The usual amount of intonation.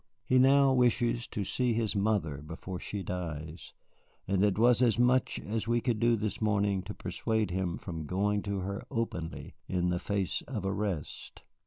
Yes: average, 4.2 semitones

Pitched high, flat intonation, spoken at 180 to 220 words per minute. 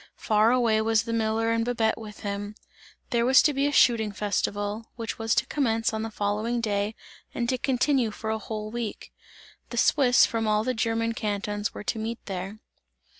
Yes: high, 225 Hz; narrow, 1.8 semitones; average, 190 wpm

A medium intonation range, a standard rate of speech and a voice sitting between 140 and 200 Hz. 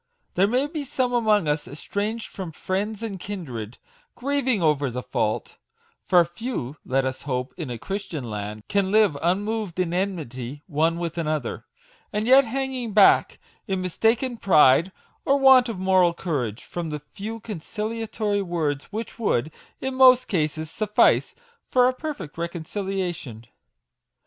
No: wide, 6.6 semitones; average, 145 wpm; high, 190 Hz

